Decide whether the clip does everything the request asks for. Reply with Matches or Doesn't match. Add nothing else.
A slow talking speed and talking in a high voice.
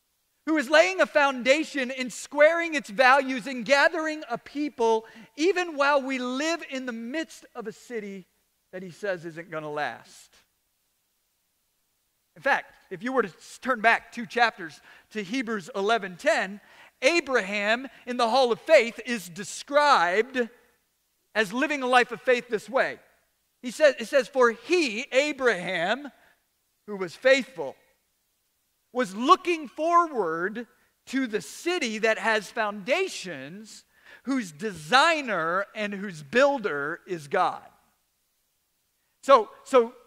Matches